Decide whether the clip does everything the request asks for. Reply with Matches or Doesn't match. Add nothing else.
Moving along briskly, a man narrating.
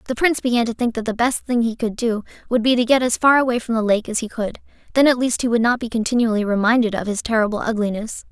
Doesn't match